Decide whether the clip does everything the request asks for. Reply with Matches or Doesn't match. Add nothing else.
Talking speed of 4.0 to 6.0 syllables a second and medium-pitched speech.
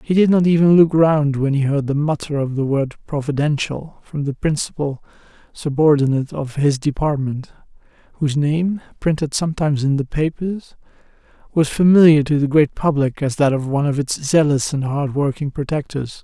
Matches